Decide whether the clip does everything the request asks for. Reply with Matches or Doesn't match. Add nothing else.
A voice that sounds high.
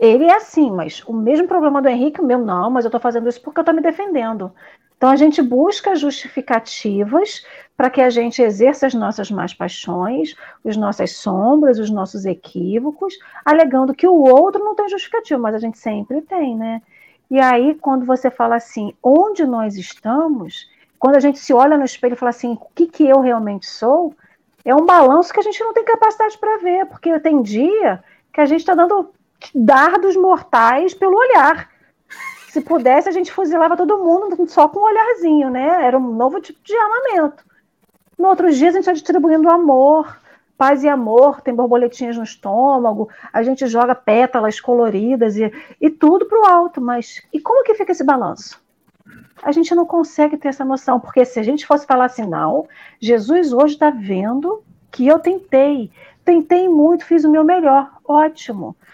Matches